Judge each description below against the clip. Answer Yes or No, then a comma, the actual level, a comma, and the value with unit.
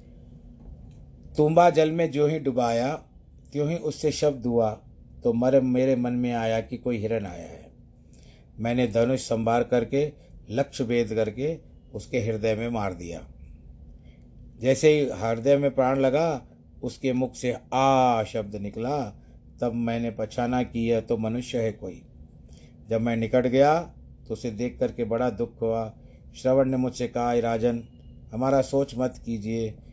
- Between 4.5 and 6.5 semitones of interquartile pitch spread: No, average, 2.7 semitones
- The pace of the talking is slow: No, average, 145 wpm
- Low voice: Yes, low, 120 Hz